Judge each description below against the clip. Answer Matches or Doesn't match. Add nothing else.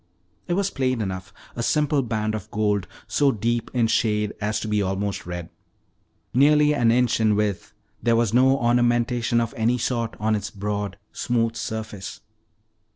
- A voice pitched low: Matches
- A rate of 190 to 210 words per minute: Doesn't match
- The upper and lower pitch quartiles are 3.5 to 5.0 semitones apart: Doesn't match